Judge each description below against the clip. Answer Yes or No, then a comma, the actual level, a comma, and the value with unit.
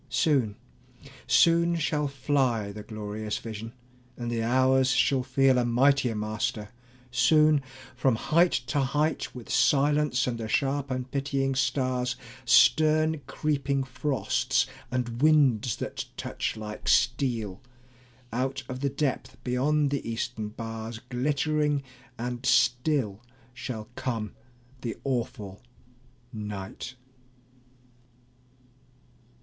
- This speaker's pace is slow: Yes, slow, 105 wpm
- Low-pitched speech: Yes, low, 130 Hz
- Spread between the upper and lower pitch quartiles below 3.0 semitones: No, average, 3.6 semitones